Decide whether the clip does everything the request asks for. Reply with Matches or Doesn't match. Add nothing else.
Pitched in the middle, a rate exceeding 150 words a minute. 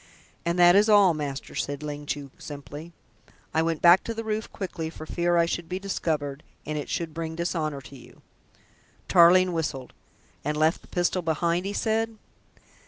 Matches